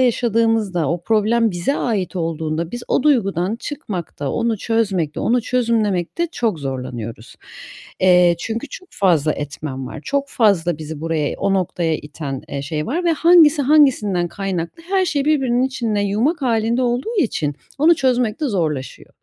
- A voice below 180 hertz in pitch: No, high, 210 Hz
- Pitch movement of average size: No, wide, 7.4 semitones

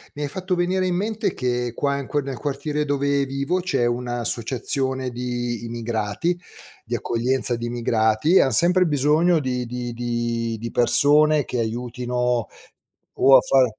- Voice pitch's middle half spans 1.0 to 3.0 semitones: No, average, 3.7 semitones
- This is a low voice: Yes, low, 130 Hz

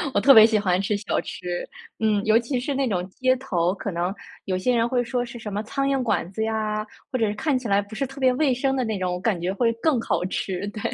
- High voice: Yes, high, 220 Hz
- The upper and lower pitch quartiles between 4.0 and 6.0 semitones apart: Yes, average, 4.5 semitones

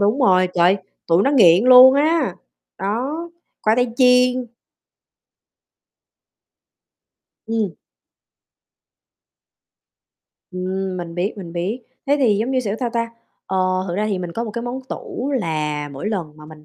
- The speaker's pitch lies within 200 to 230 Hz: Yes, high, 210 Hz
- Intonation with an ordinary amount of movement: No, wide, 5.9 semitones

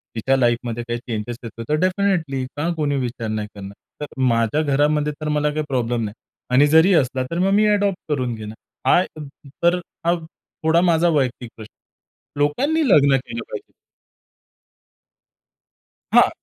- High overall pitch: No, medium, 140 Hz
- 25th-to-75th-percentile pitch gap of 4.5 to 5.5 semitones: Yes, average, 5.2 semitones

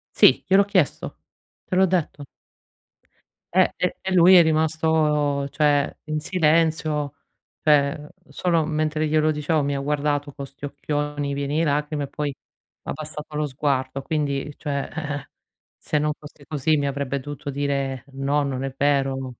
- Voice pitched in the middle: Yes, medium, 150 Hz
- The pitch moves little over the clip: Yes, narrow, 1.7 semitones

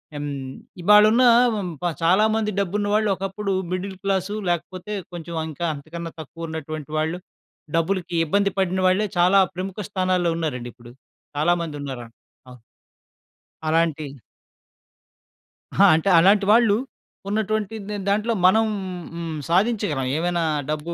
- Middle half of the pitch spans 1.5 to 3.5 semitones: No, average, 4.0 semitones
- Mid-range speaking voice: Yes, medium, 180 Hz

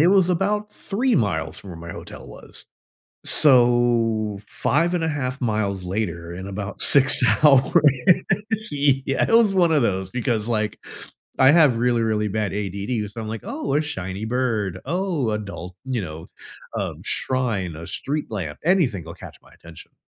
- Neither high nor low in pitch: No, low, 115 Hz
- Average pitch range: No, wide, 6.7 semitones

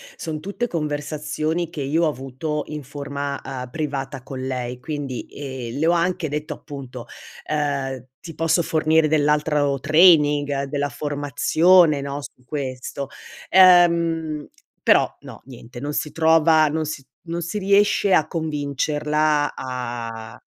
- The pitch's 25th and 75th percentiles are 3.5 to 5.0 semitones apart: No, narrow, 2.6 semitones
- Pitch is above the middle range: No, medium, 150 Hz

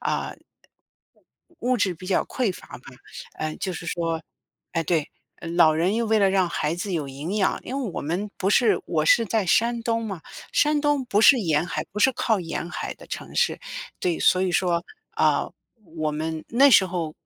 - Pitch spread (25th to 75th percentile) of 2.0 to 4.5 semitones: No, average, 5.2 semitones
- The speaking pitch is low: No, medium, 185 Hz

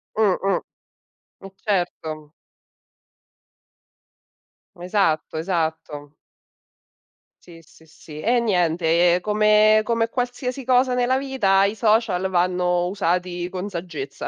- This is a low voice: No, medium, 185 Hz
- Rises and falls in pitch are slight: No, average, 4.3 semitones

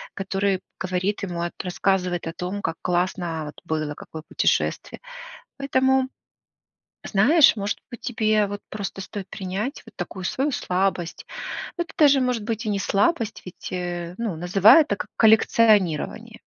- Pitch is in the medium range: No, high, 195 Hz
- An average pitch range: Yes, average, 4.0 semitones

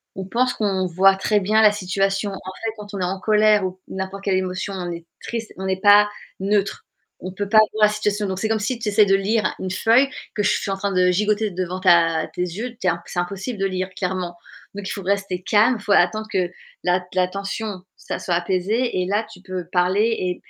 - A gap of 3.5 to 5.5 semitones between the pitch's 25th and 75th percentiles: No, narrow, 2.4 semitones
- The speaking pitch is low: No, high, 195 Hz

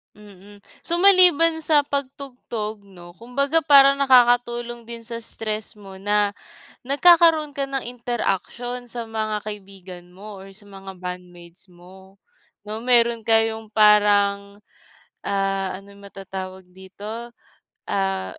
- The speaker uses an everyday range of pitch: Yes, average, 4.0 semitones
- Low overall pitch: No, high, 215 Hz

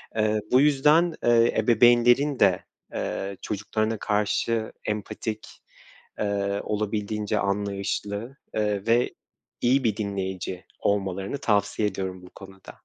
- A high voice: No, low, 105 Hz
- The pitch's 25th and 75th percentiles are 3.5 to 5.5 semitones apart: No, average, 2.7 semitones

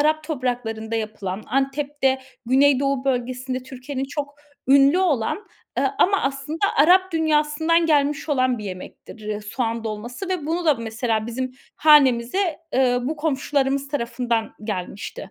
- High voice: Yes, very high, 270 Hz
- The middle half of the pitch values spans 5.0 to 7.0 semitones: No, average, 4.1 semitones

